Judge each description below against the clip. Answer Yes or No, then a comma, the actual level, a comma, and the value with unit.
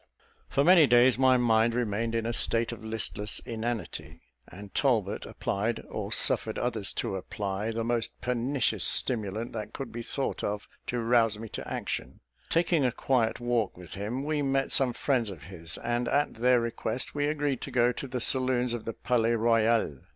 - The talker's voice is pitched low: Yes, low, 115 Hz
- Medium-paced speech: Yes, average, 180 wpm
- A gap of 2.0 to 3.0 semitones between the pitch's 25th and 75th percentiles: Yes, narrow, 2.5 semitones